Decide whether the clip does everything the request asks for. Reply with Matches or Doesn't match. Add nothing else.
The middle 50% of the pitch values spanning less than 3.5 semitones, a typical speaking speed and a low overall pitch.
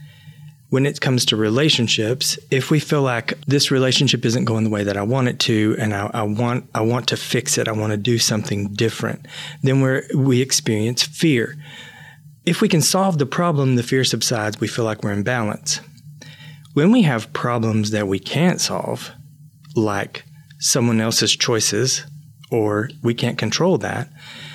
Doesn't match